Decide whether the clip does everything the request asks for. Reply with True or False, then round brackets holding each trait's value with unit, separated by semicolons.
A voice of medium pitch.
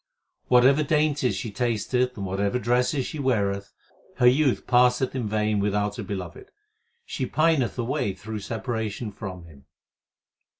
False (120 Hz)